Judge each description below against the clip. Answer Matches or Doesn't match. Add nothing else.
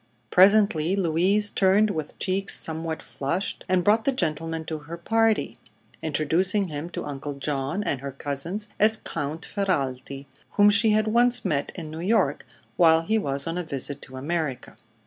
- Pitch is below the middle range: Doesn't match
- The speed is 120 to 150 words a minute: Doesn't match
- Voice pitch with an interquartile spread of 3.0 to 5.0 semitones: Doesn't match